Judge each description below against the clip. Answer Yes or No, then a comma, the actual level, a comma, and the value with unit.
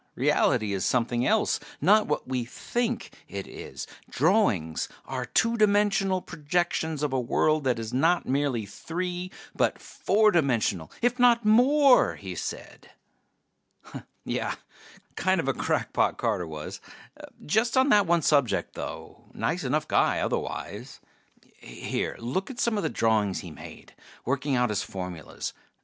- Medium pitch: Yes, medium, 150 Hz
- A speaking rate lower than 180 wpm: Yes, average, 140 wpm